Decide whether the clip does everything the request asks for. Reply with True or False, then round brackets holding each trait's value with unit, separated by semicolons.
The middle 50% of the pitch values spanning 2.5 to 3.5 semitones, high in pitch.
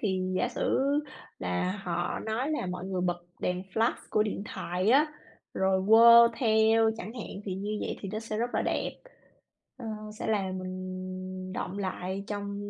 True (3.2 semitones; 205 Hz)